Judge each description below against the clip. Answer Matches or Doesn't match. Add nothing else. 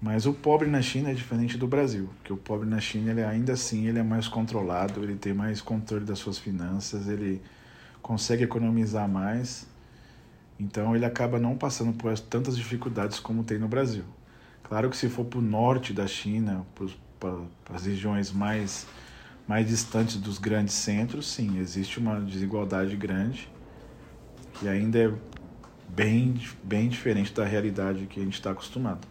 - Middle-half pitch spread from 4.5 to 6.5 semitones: Doesn't match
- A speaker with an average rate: Matches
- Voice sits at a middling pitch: Doesn't match